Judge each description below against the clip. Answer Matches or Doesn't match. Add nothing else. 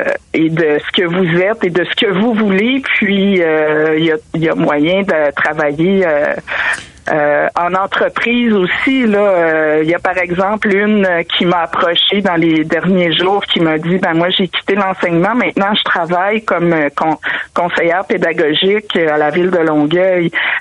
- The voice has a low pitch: Doesn't match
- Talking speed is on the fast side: Doesn't match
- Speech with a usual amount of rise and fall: Matches